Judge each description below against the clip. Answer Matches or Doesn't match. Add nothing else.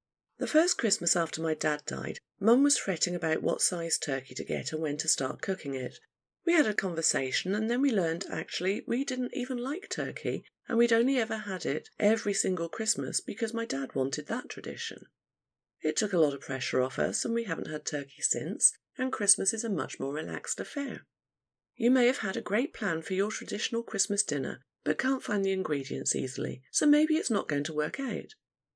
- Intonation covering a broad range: Matches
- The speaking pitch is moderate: Doesn't match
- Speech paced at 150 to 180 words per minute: Doesn't match